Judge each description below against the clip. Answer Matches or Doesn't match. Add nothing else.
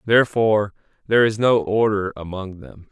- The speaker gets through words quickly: Doesn't match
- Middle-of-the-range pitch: Doesn't match